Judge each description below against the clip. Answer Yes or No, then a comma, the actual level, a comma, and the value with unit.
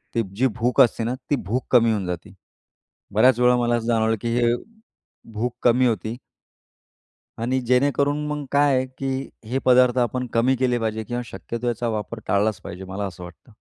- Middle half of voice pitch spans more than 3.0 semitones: No, narrow, 2.5 semitones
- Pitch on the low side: Yes, low, 120 Hz